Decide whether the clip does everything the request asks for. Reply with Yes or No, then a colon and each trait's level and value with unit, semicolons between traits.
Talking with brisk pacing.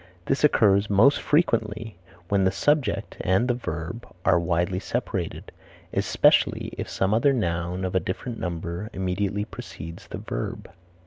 No: average, 140 wpm